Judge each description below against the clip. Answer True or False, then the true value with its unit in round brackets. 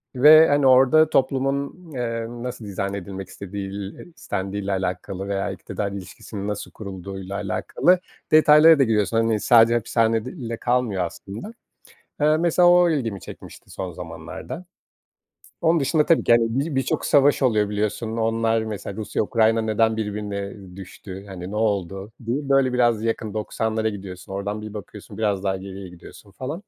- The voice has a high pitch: False (110 Hz)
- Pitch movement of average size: True (4.6 semitones)